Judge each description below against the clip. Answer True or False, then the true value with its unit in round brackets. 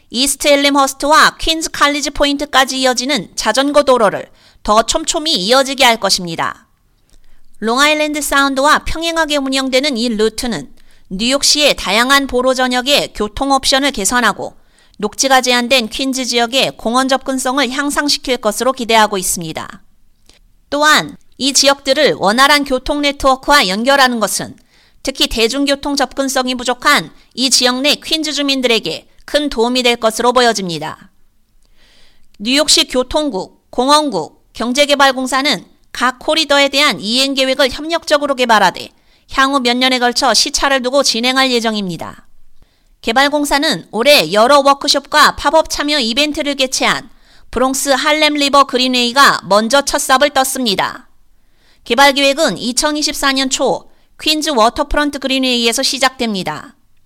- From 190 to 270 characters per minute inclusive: False (320 characters per minute)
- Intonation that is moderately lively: True (3.0 semitones)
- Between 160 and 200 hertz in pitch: False (270 Hz)